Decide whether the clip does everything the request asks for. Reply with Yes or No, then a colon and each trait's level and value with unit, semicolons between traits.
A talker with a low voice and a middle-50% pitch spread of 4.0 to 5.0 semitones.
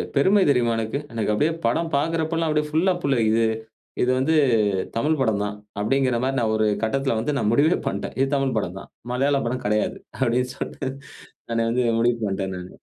Yes: low, 125 Hz; average, 4.3 semitones